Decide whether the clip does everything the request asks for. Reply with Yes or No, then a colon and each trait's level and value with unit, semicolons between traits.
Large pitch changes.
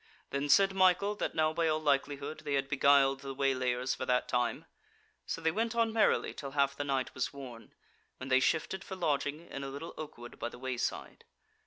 No: average, 3.4 semitones